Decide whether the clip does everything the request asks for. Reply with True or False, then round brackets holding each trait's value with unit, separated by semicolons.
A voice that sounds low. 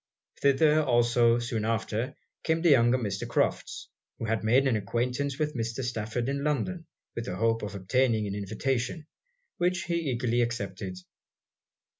True (120 Hz)